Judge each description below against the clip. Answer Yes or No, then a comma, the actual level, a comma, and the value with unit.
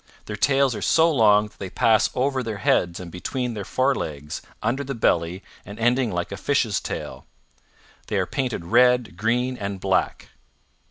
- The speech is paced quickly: No, average, 170 wpm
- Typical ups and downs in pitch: Yes, average, 4.8 semitones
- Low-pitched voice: Yes, low, 115 Hz